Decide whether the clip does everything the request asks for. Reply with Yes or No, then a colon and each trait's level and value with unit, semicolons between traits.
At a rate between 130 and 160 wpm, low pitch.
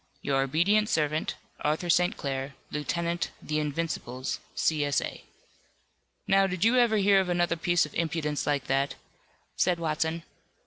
No: average, 145 wpm; medium, 165 Hz